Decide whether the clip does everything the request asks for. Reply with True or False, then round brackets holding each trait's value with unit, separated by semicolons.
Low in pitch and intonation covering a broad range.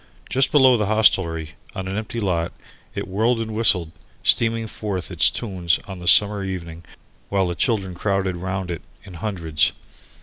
False (95 Hz; 3.8 semitones)